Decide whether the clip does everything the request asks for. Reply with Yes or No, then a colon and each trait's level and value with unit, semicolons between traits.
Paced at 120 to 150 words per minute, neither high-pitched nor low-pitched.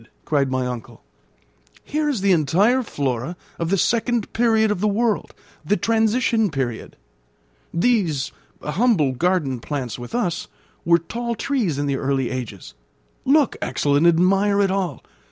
Yes: average, 145 wpm; medium, 180 Hz